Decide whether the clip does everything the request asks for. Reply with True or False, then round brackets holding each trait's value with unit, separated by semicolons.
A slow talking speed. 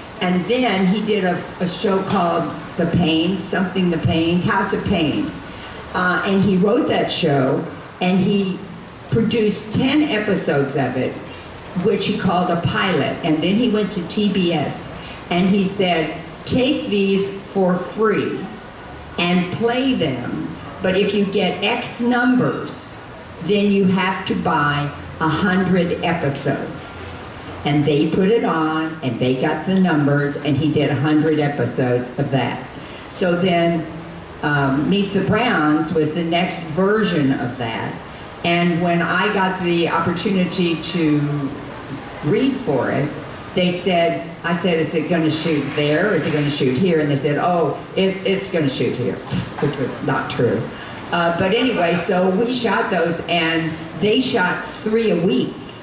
False (160 wpm)